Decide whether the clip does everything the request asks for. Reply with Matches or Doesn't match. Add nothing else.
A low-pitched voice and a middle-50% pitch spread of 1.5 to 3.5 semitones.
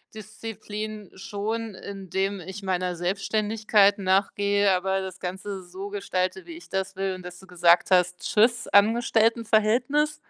Doesn't match